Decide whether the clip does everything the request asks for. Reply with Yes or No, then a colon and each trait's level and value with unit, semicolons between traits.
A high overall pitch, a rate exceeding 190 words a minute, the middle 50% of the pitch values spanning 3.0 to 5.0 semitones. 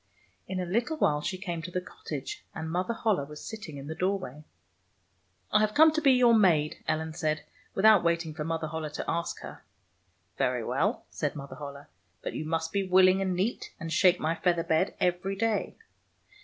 No: medium, 175 Hz; fast, 205 wpm; average, 3.7 semitones